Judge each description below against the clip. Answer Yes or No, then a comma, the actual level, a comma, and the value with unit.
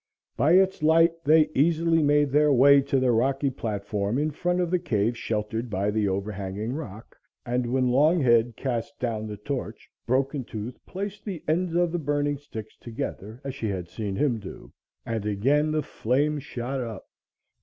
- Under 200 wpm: Yes, average, 175 wpm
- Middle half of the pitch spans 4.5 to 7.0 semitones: Yes, average, 5.3 semitones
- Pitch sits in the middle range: No, low, 130 Hz